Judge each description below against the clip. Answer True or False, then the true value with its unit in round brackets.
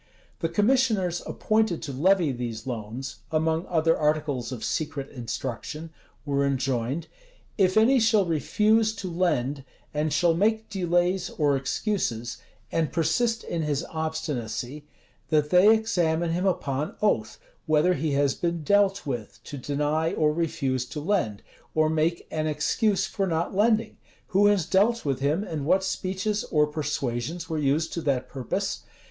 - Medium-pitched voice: True (160 Hz)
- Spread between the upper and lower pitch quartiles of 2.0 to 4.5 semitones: False (5.1 semitones)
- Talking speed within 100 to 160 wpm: True (150 wpm)